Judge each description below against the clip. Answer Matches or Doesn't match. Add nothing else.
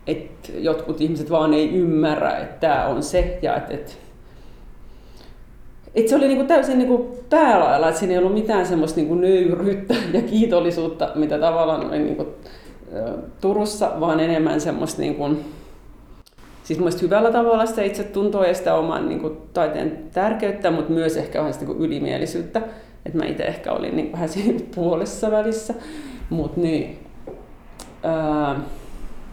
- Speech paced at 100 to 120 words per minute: Doesn't match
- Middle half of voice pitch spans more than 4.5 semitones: Matches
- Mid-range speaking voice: Matches